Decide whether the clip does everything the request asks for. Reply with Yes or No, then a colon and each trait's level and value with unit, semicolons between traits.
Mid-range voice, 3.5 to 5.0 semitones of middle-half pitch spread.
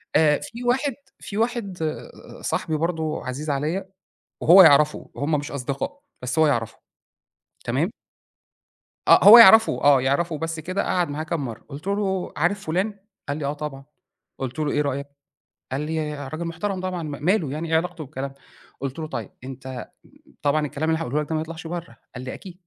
Yes: medium, 155 Hz; average, 4.0 semitones